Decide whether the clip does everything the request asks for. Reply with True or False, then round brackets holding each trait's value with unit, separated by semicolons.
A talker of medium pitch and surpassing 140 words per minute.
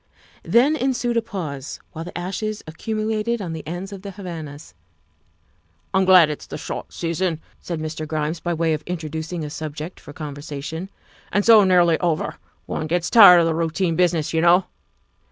True (170 Hz; 175 wpm)